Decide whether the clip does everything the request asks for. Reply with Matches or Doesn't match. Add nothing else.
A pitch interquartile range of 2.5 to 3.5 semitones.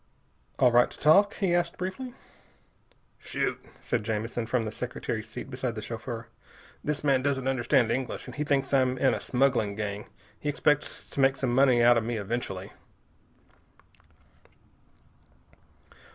Matches